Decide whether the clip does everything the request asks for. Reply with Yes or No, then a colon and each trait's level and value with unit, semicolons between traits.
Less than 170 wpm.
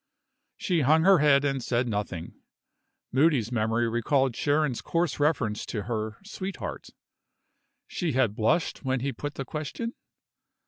Yes: slow, 135 wpm